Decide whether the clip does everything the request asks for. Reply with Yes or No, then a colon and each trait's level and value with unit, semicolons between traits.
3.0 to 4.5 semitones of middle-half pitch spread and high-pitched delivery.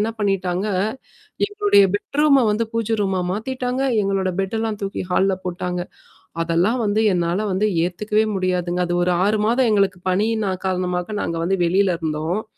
Yes: average, 3.3 semitones; high, 195 Hz